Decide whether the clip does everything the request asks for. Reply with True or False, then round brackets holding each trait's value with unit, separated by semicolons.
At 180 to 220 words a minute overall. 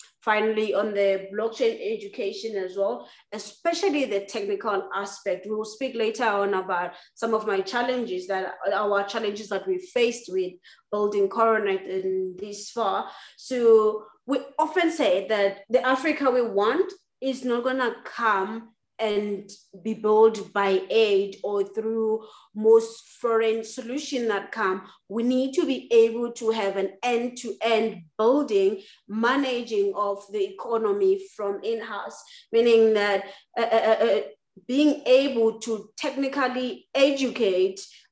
False (135 wpm)